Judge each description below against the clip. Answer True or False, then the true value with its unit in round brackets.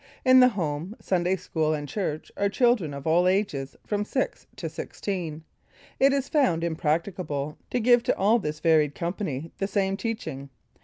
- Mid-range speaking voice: True (180 Hz)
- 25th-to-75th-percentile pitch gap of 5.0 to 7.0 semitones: True (5.4 semitones)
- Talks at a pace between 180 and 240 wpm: False (165 wpm)